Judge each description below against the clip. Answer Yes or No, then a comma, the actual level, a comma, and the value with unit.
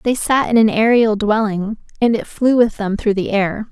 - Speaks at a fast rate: Yes, fast, 225 wpm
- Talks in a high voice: Yes, high, 220 Hz